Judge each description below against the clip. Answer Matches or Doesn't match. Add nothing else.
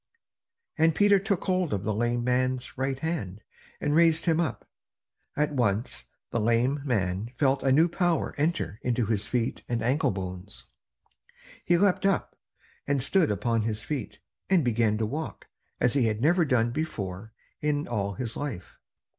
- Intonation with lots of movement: Matches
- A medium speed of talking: Matches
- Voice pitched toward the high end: Doesn't match